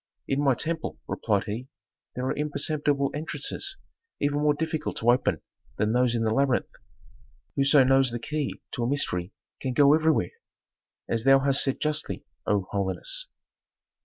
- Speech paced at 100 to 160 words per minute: Yes, average, 155 wpm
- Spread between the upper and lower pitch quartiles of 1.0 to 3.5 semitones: No, average, 3.9 semitones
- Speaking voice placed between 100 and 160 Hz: Yes, low, 135 Hz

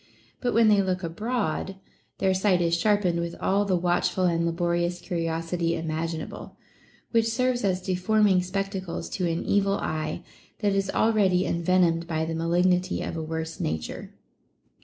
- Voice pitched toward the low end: No, medium, 180 Hz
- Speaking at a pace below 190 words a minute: Yes, average, 150 wpm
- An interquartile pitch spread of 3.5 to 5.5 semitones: No, average, 2.9 semitones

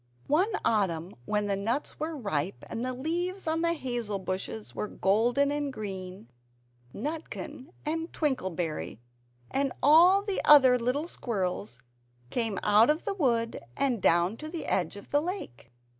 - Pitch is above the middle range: Yes, high, 245 Hz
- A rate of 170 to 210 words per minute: No, average, 150 wpm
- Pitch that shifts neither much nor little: No, wide, 7.6 semitones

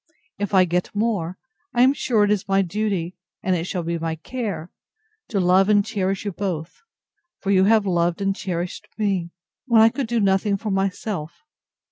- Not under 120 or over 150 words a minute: No, average, 185 wpm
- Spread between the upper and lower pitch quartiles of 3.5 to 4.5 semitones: No, average, 3.0 semitones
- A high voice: Yes, high, 195 Hz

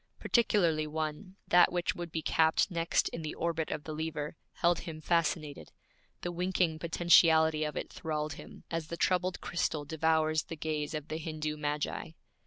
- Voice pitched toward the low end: No, medium, 160 Hz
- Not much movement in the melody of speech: Yes, narrow, 1.8 semitones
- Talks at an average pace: Yes, average, 170 wpm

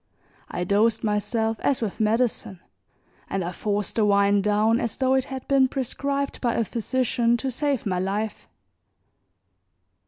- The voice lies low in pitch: No, high, 225 Hz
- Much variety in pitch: No, average, 3.8 semitones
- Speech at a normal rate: Yes, average, 150 wpm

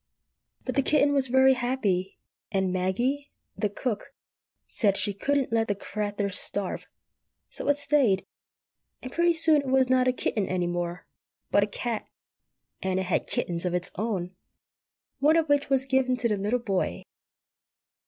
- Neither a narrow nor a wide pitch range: No, wide, 5.7 semitones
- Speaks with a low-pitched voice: No, high, 230 Hz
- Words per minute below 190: Yes, average, 165 wpm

